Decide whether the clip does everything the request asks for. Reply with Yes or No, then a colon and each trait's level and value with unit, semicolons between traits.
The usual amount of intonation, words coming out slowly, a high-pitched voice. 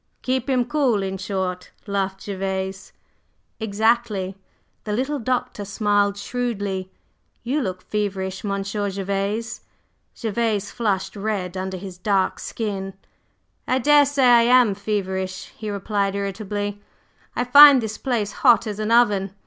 Yes: average, 3.2 semitones; slow, 125 wpm; high, 205 Hz